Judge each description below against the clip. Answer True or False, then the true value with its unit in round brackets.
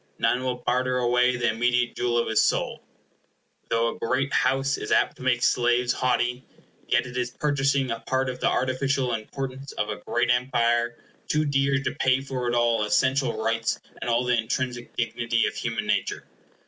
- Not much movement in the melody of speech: True (1.7 semitones)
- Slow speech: False (185 wpm)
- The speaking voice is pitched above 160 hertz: False (125 Hz)